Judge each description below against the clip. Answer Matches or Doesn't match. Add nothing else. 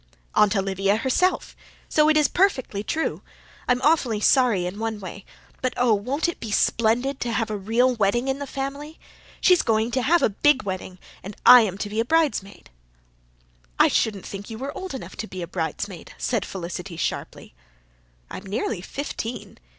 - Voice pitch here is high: Matches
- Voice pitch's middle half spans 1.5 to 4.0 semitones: Doesn't match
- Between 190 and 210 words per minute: Doesn't match